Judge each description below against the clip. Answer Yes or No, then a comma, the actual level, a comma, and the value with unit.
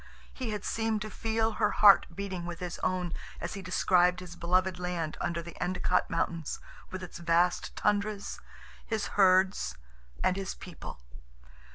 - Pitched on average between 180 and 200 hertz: Yes, medium, 185 Hz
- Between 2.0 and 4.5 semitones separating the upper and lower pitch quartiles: Yes, narrow, 2.6 semitones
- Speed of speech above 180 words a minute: No, average, 155 wpm